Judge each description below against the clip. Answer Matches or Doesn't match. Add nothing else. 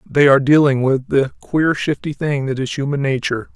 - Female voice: Doesn't match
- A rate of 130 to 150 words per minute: Doesn't match